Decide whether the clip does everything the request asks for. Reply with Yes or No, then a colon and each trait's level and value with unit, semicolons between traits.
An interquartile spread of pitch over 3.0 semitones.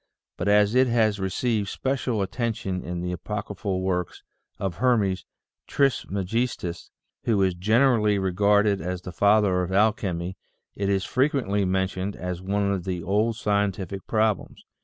No: average, 2.7 semitones